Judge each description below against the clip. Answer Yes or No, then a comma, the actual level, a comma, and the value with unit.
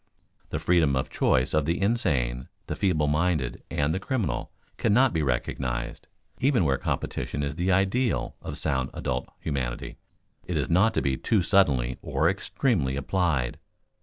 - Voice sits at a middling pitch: No, very low, 75 Hz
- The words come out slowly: No, average, 155 wpm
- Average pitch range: No, wide, 6.5 semitones